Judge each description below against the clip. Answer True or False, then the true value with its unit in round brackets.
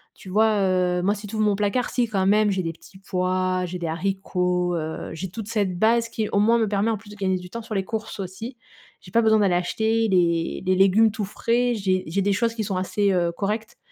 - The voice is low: False (200 Hz)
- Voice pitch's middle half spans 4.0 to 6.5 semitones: False (3.1 semitones)